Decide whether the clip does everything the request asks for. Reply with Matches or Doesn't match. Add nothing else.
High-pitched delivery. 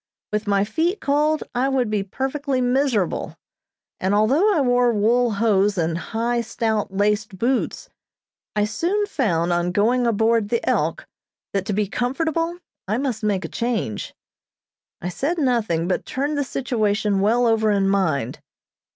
Matches